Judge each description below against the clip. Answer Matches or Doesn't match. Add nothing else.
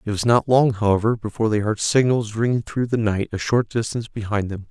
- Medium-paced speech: Doesn't match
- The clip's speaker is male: Matches